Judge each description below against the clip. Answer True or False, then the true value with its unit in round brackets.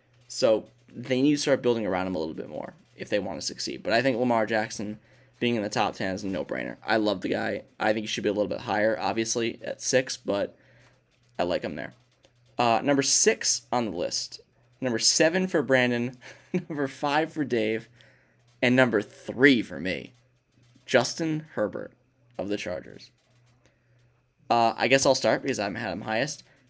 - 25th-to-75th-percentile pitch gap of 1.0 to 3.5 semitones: True (2.7 semitones)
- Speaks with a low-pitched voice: True (125 Hz)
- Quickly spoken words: False (190 wpm)